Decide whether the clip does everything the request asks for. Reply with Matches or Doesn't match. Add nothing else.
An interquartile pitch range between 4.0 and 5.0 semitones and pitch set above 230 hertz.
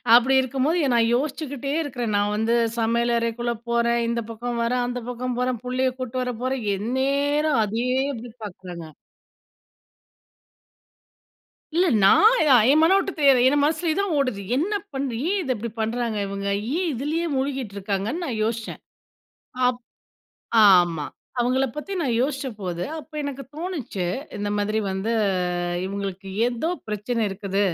Matches